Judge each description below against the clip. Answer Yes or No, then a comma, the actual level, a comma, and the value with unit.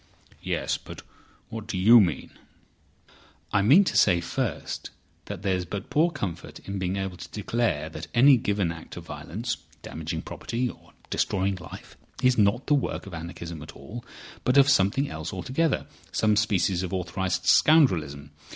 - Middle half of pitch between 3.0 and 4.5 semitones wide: No, wide, 5.4 semitones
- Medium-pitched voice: No, very low, 95 Hz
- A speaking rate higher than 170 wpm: No, average, 150 wpm